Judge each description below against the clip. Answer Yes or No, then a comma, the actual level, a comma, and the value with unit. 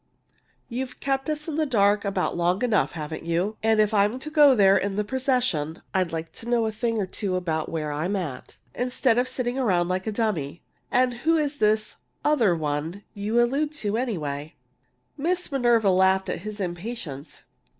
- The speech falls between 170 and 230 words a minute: Yes, average, 190 wpm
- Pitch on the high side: Yes, high, 210 Hz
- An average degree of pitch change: No, wide, 5.9 semitones